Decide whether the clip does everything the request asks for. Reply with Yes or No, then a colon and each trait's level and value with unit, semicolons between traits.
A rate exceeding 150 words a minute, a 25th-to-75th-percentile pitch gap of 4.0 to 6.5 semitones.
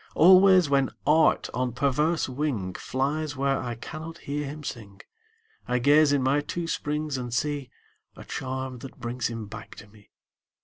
No: average, 165 wpm; average, 3.3 semitones